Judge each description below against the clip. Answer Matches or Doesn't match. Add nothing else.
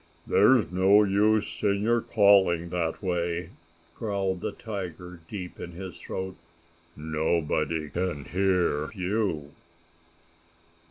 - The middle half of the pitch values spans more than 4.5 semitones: Doesn't match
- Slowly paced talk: Matches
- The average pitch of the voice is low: Matches